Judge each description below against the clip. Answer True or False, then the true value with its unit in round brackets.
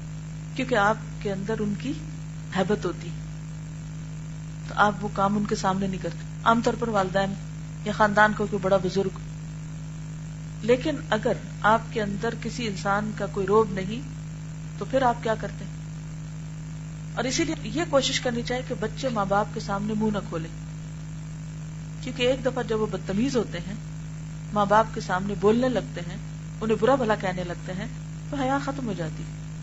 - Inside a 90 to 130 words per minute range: False (170 wpm)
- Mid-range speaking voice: True (165 Hz)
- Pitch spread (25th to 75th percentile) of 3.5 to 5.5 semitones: True (4.7 semitones)